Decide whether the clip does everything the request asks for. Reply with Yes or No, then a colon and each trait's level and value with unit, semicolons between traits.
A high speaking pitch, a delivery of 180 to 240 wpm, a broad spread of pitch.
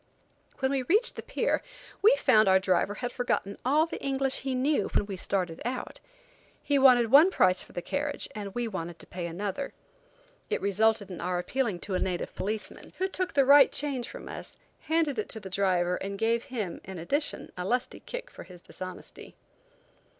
Yes: high, 220 Hz; average, 195 wpm; wide, 6.6 semitones